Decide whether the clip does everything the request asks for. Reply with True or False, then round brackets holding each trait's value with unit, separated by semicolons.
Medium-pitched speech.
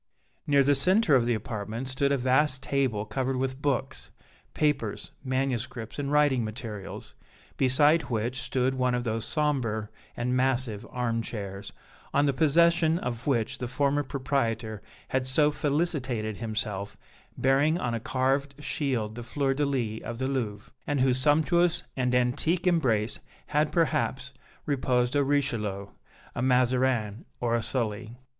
False (130 Hz)